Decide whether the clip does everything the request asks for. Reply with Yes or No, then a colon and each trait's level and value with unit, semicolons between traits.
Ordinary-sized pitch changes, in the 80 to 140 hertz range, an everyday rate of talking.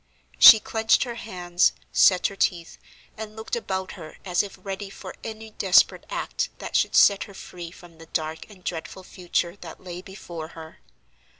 No: average, 3.2 semitones; medium, 185 Hz; average, 175 wpm